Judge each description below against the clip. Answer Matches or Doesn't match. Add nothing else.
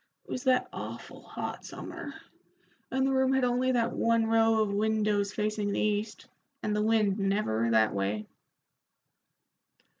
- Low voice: Doesn't match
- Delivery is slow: Doesn't match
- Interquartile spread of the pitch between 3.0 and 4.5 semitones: Doesn't match